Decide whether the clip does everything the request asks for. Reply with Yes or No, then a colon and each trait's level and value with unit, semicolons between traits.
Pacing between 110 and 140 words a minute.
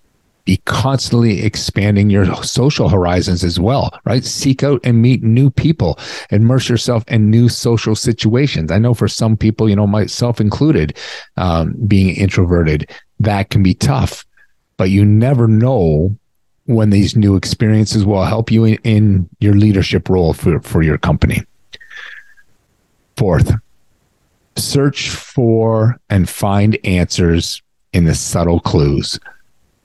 Yes: slow, 135 wpm